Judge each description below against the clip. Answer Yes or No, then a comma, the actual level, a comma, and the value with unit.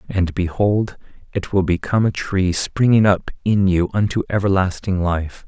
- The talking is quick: No, average, 155 wpm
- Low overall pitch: Yes, very low, 95 Hz